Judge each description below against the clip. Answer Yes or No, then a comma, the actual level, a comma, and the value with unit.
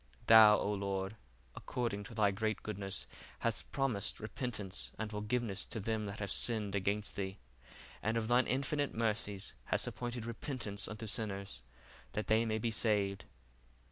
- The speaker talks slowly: No, average, 150 wpm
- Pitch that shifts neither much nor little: No, narrow, 2.3 semitones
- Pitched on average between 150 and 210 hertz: No, low, 105 Hz